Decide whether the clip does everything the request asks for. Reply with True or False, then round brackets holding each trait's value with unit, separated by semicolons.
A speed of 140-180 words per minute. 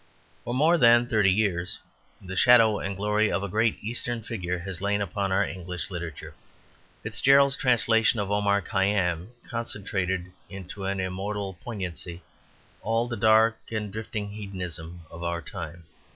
True (145 wpm)